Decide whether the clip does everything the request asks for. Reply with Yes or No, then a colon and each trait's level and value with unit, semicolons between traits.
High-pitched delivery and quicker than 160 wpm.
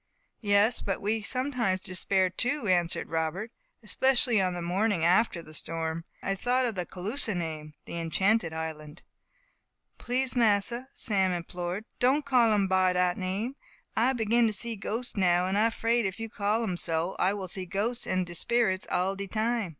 Yes: high, 195 Hz; average, 175 wpm